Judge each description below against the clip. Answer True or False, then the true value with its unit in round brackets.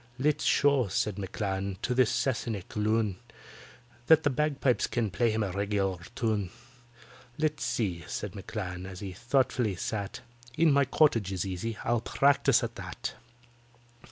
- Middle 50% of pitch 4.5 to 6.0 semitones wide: True (5.1 semitones)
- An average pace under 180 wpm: True (140 wpm)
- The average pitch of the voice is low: True (110 Hz)